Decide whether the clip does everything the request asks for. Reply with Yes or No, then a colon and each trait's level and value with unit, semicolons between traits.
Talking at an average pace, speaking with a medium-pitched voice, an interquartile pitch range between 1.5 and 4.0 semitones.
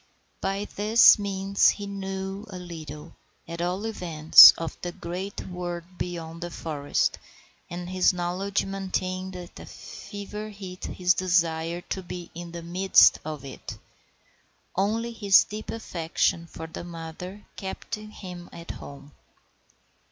No: slow, 130 wpm; medium, 180 Hz; narrow, 2.5 semitones